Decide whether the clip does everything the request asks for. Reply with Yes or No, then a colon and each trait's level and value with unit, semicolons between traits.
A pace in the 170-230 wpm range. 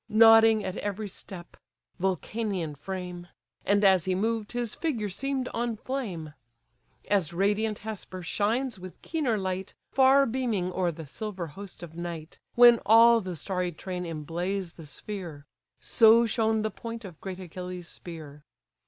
No: average, 145 wpm